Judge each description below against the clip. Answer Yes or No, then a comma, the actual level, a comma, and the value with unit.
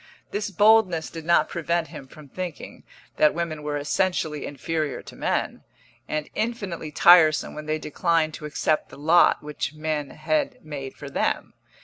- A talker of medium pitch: Yes, medium, 155 Hz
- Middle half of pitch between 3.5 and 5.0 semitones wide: No, narrow, 2.5 semitones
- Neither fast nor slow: Yes, average, 155 wpm